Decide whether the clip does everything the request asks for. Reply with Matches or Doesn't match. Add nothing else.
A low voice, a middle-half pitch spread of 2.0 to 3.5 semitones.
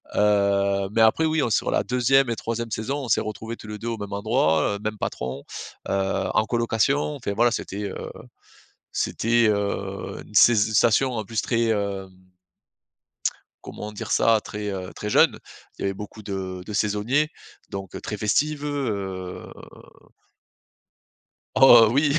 Matches